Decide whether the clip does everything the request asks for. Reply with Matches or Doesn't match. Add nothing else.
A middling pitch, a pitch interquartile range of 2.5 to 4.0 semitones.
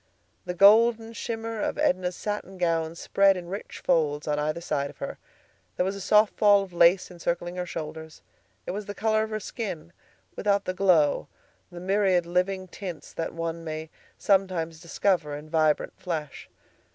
Matches